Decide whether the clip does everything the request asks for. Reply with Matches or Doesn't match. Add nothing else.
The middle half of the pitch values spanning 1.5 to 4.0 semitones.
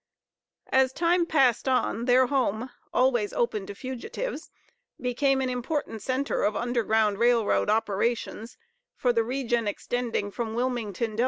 Matches